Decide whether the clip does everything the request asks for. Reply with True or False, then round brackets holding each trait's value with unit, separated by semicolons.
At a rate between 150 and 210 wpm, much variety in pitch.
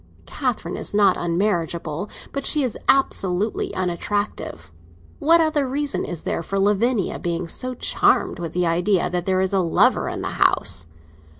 False (160 wpm; 4.8 semitones)